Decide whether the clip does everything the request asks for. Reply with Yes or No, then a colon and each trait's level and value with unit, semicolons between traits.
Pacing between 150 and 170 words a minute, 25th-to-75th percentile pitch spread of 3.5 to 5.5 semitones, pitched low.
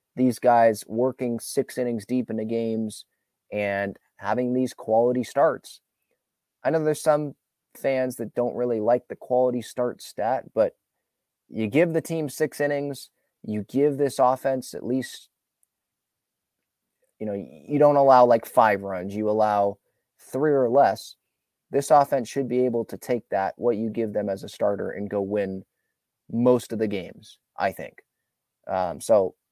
Yes: average, 160 wpm; average, 3.8 semitones; low, 125 Hz